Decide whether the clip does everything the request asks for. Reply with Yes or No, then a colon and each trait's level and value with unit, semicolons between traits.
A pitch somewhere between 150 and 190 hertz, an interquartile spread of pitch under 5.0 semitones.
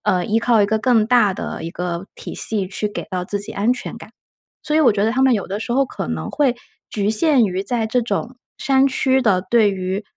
No: high, 220 Hz; average, 4.0 semitones